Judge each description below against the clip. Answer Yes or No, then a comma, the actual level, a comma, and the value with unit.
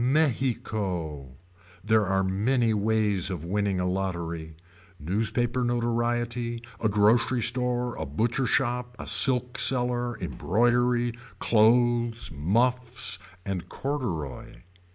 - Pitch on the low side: Yes, low, 115 Hz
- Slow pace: Yes, slow, 100 wpm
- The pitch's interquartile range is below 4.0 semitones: No, average, 4.3 semitones